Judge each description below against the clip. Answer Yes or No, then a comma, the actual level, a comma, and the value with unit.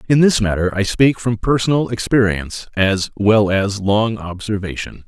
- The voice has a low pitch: Yes, low, 105 Hz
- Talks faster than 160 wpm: No, average, 155 wpm